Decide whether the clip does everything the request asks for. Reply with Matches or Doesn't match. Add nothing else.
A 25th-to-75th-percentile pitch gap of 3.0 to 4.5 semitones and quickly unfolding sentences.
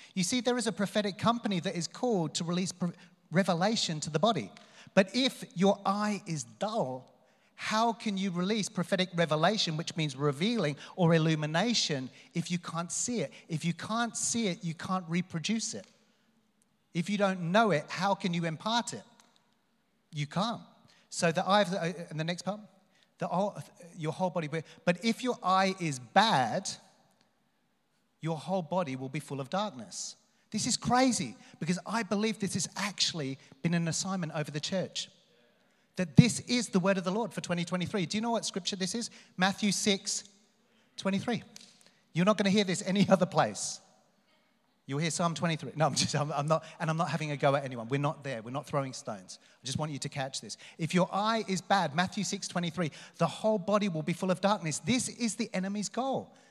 Doesn't match